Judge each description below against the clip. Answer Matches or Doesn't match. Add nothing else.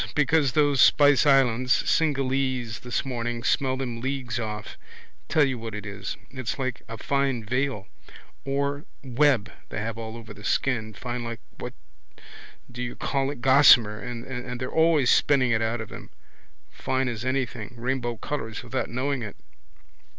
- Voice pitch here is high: Doesn't match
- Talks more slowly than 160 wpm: Doesn't match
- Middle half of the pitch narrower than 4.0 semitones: Matches